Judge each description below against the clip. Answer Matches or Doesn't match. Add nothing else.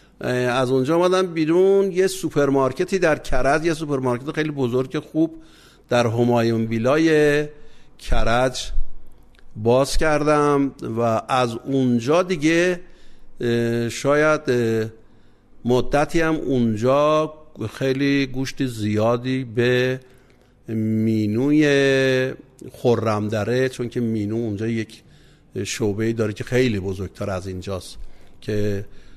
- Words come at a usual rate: Doesn't match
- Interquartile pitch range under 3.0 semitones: Doesn't match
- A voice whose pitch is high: Doesn't match